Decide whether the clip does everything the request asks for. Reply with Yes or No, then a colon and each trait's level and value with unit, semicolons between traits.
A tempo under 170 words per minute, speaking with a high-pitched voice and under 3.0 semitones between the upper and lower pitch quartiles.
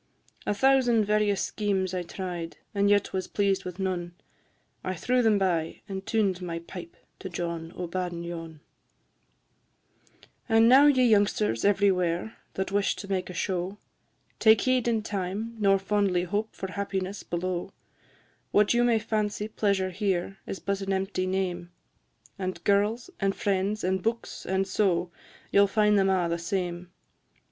Yes: average, 155 wpm; high, 195 Hz; narrow, 2.5 semitones